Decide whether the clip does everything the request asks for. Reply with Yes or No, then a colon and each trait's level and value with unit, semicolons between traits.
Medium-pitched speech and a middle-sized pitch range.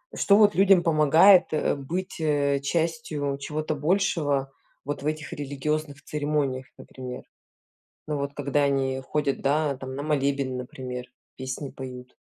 No: medium, 145 Hz; narrow, 2.3 semitones